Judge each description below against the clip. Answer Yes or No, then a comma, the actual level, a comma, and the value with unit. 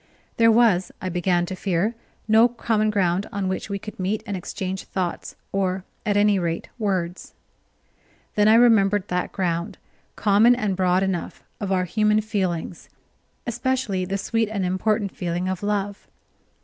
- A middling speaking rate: Yes, average, 155 wpm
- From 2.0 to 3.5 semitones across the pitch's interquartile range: Yes, average, 2.7 semitones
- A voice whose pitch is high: Yes, high, 195 Hz